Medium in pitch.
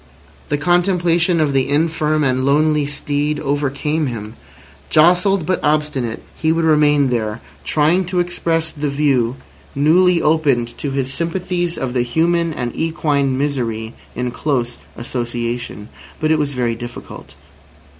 Yes: medium, 145 Hz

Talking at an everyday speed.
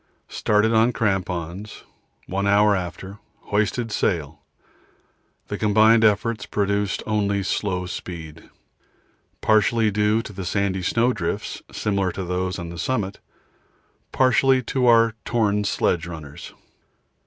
No: slow, 110 wpm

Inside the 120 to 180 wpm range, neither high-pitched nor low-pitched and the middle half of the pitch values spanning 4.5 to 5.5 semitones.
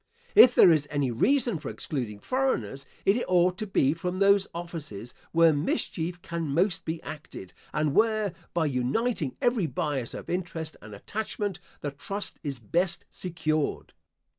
Yes: average, 150 wpm; medium, 165 Hz; average, 5.1 semitones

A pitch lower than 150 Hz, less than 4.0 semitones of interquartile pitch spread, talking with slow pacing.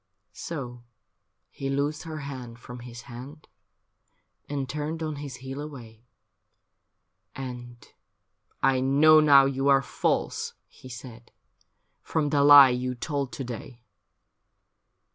Yes: low, 135 Hz; average, 2.7 semitones; slow, 125 wpm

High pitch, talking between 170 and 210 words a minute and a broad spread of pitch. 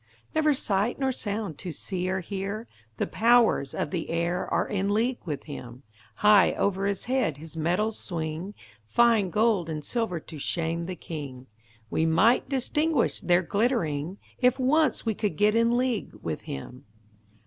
No: high, 195 Hz; average, 160 wpm; wide, 6.1 semitones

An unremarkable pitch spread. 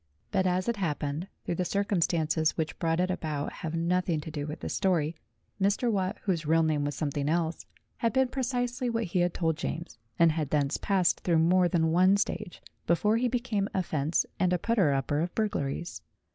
Yes: average, 3.9 semitones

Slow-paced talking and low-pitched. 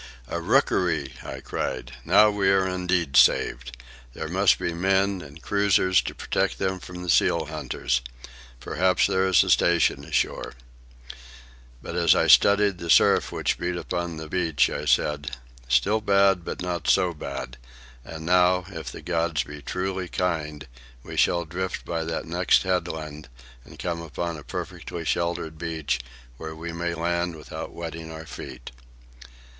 No: average, 155 wpm; very low, 85 Hz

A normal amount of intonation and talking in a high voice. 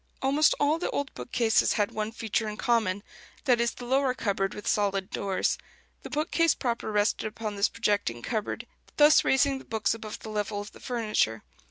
Yes: average, 3.7 semitones; high, 220 Hz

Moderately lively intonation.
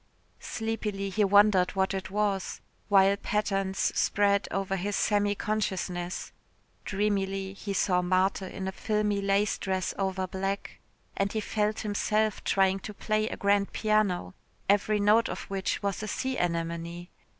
No: narrow, 1.6 semitones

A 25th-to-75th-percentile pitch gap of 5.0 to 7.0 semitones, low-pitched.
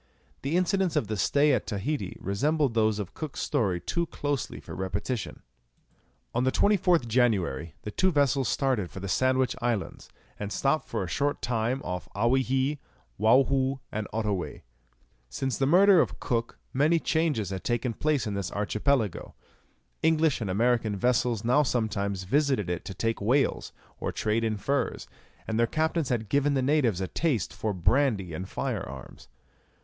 Yes: wide, 5.5 semitones; low, 120 Hz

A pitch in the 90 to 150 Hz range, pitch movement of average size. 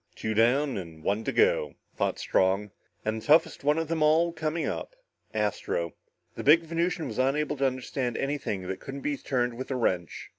No: low, 135 Hz; wide, 6.2 semitones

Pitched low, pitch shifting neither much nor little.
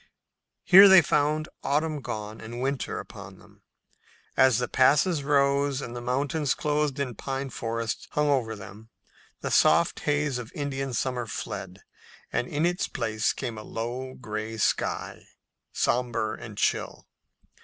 Yes: low, 130 Hz; average, 4.0 semitones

